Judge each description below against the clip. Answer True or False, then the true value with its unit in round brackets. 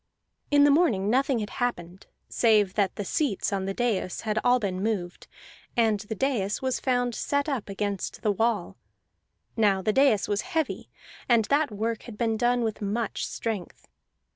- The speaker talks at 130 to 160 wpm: False (170 wpm)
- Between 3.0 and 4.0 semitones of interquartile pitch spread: True (3.5 semitones)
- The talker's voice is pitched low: False (220 Hz)